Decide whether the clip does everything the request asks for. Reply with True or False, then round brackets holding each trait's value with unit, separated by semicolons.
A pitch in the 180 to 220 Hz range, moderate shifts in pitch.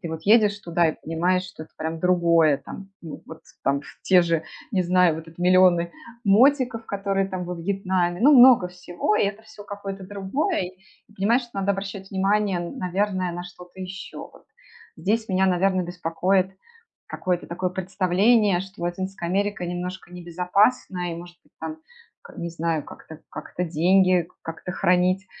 False (185 Hz; 2.3 semitones)